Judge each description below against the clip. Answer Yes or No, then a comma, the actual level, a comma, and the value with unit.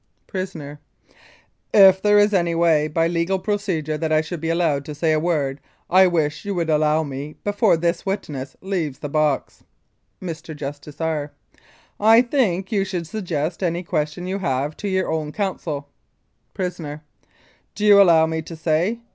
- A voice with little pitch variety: No, average, 3.8 semitones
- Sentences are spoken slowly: No, average, 165 wpm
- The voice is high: No, medium, 165 Hz